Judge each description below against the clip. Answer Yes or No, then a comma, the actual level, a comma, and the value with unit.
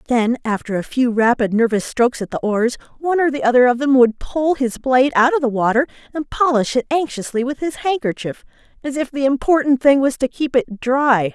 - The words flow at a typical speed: No, fast, 215 wpm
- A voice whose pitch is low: No, very high, 255 Hz